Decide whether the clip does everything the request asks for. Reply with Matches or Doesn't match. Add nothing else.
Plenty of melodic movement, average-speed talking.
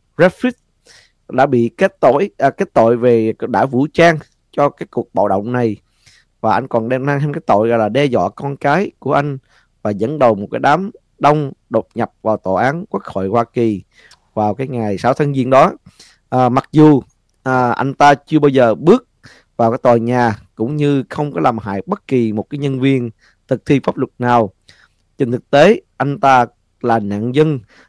Doesn't match